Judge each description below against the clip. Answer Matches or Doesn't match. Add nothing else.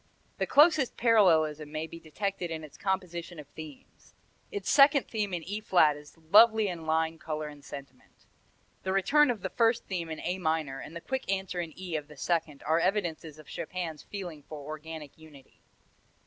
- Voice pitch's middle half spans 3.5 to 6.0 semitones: Matches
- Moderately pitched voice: Matches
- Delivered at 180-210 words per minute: Matches